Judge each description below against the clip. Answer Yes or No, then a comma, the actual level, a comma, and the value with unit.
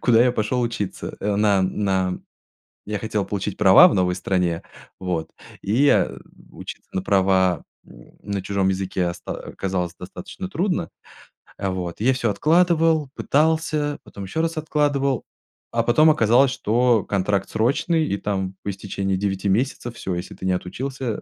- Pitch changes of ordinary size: No, wide, 5.9 semitones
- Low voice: Yes, low, 105 Hz